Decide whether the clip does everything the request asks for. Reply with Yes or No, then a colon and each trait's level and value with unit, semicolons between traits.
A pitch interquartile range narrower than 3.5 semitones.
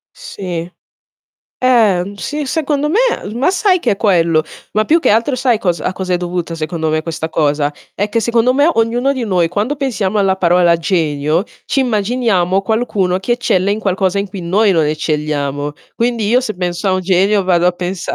No: average, 5.1 semitones